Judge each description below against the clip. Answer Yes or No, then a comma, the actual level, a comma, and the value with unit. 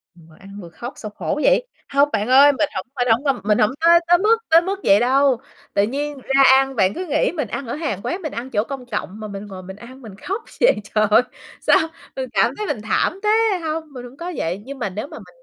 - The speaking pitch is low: No, very high, 265 Hz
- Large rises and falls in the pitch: Yes, wide, 6.9 semitones